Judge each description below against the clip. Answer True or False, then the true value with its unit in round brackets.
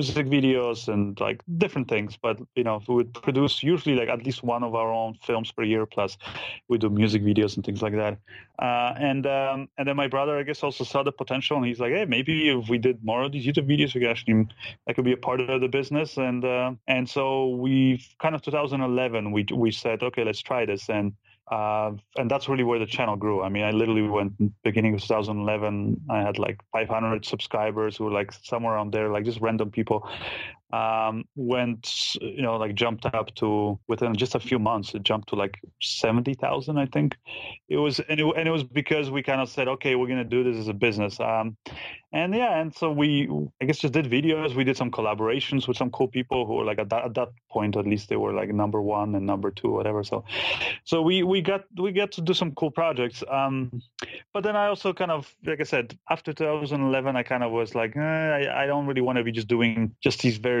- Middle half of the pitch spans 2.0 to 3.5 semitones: False (4.2 semitones)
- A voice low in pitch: True (125 Hz)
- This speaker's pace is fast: True (235 wpm)